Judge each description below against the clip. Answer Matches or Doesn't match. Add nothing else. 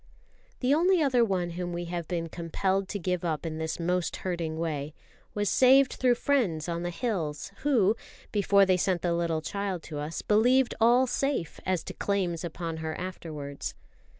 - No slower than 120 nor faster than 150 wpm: Doesn't match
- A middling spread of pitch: Matches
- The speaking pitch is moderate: Matches